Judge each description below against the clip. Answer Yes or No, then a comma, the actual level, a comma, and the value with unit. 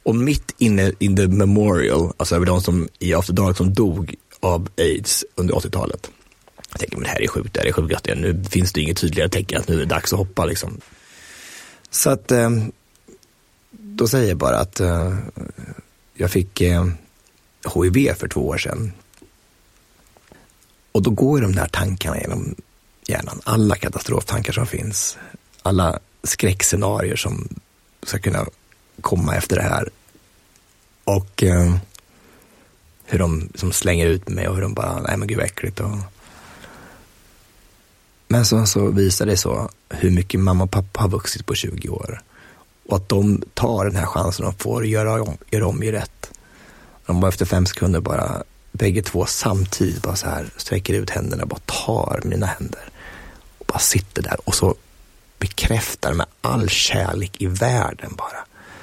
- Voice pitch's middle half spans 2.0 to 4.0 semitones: Yes, average, 3.4 semitones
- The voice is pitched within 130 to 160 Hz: No, very low, 95 Hz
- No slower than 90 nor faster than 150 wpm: No, average, 165 wpm